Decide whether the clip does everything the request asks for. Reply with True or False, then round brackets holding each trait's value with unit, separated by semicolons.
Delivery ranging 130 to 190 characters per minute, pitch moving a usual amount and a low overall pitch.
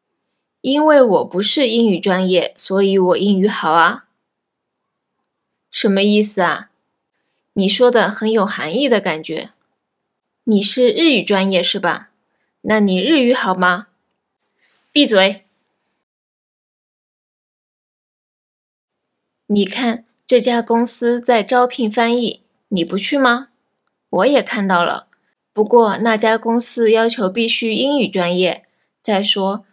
False (170 characters per minute; 3.8 semitones; 215 Hz)